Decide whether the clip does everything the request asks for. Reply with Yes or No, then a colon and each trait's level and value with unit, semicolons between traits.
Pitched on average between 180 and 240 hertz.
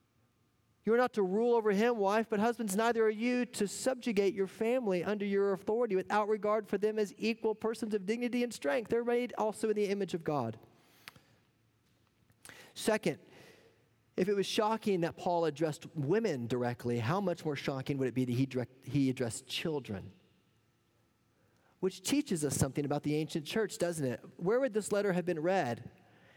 Yes: medium, 185 Hz